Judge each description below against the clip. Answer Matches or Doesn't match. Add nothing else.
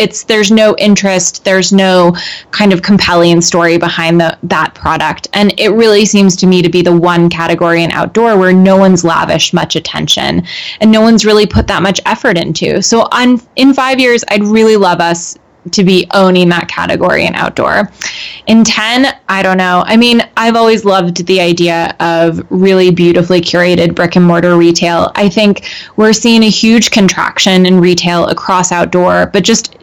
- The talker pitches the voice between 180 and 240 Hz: Matches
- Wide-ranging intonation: Doesn't match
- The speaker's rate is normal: Matches